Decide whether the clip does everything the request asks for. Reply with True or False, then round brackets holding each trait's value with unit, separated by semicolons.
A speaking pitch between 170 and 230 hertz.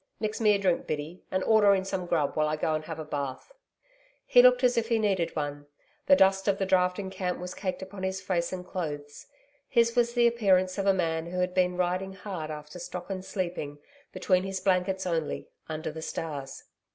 True (185 Hz)